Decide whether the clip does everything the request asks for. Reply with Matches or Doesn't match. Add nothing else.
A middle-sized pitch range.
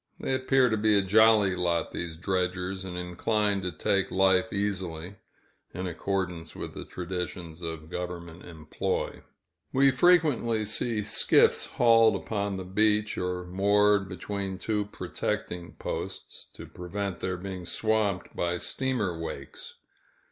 Matches